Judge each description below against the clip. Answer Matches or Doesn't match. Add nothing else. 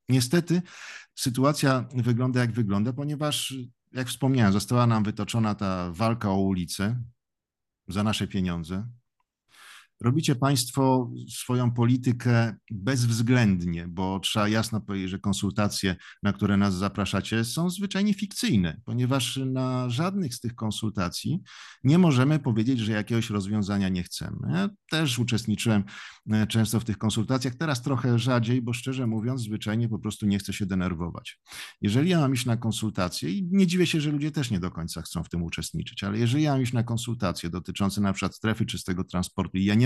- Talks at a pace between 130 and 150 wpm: Doesn't match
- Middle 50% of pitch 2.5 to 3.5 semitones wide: Doesn't match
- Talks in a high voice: Doesn't match